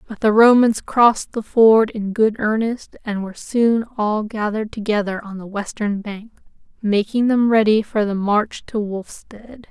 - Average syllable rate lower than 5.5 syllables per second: Yes, 4.4 syllables/s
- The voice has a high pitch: Yes, high, 215 Hz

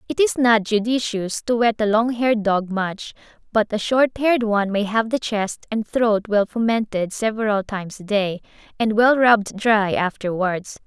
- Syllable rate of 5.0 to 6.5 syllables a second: No, 4.8 syllables/s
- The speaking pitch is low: No, high, 215 Hz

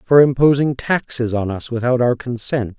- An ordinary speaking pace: Yes, average, 170 wpm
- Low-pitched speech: Yes, low, 125 Hz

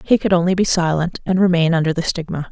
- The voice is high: No, medium, 170 Hz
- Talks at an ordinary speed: No, fast, 240 wpm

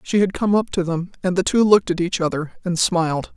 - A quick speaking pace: Yes, fast, 270 wpm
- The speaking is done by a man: No, female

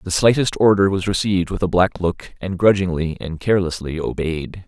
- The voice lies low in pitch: Yes, very low, 90 Hz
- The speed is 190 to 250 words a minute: No, average, 180 wpm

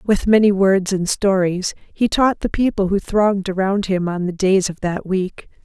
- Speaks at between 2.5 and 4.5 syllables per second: Yes, 4.4 syllables/s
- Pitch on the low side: No, high, 195 Hz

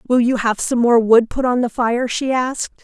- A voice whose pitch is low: No, high, 240 Hz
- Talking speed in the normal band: No, fast, 255 wpm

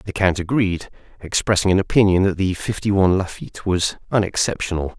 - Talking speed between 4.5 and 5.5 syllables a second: No, 6.0 syllables/s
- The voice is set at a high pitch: No, very low, 95 Hz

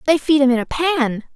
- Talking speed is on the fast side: Yes, fast, 265 wpm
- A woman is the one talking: Yes, female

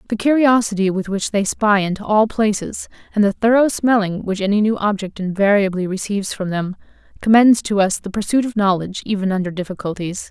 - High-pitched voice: Yes, high, 205 Hz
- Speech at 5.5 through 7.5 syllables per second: Yes, 5.8 syllables/s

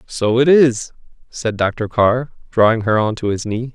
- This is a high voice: No, low, 115 Hz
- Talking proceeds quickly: No, average, 190 wpm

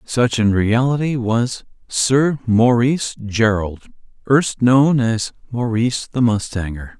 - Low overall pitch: Yes, low, 120 Hz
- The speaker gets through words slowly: Yes, slow, 105 wpm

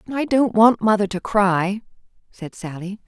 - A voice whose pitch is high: Yes, high, 205 Hz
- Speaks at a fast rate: No, average, 155 wpm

